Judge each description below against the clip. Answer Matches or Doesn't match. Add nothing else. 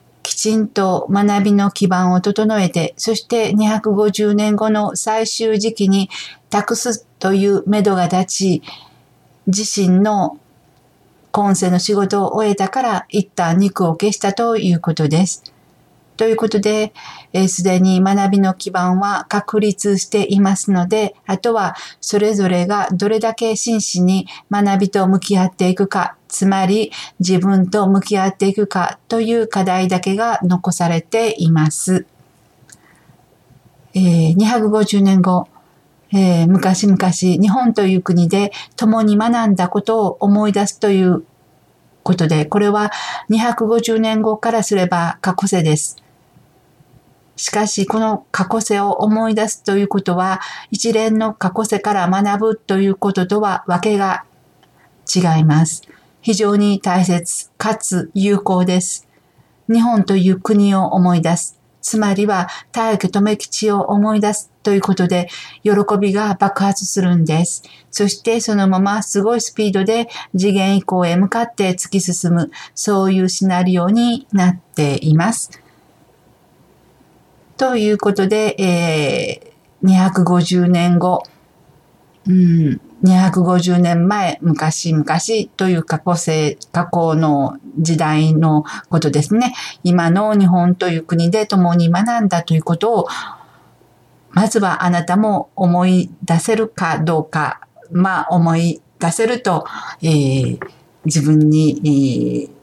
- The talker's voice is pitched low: Doesn't match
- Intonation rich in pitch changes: Doesn't match